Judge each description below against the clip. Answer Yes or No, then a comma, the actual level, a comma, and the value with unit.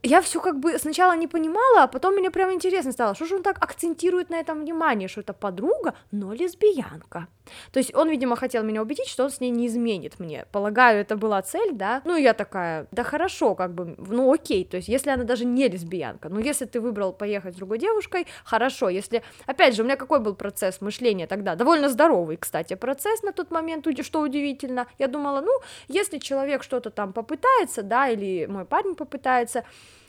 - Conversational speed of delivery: No, fast, 205 wpm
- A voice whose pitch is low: No, very high, 260 Hz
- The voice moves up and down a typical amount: No, wide, 7.5 semitones